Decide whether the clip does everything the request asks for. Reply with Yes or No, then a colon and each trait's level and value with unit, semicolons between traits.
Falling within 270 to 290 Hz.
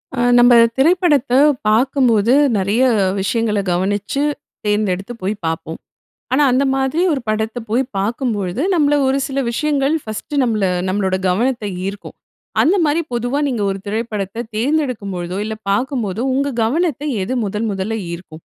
No: high, 230 Hz